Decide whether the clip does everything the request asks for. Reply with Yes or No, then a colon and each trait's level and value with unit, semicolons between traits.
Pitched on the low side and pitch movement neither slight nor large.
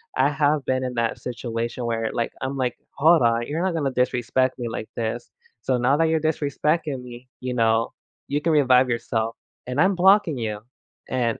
Yes: low, 130 Hz; average, 3.9 semitones